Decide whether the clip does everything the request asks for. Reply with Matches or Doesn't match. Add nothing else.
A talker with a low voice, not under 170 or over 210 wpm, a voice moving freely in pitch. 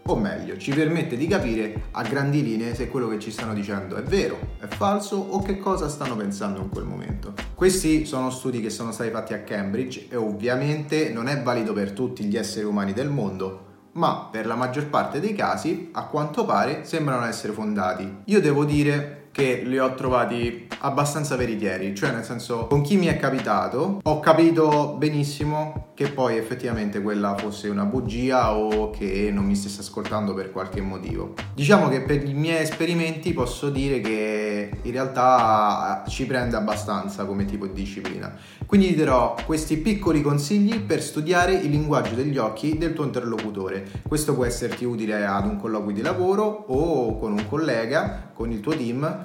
Matches